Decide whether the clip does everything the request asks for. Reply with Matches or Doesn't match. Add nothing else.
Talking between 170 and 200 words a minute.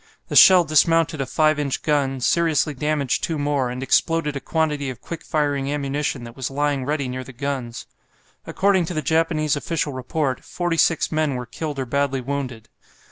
Matches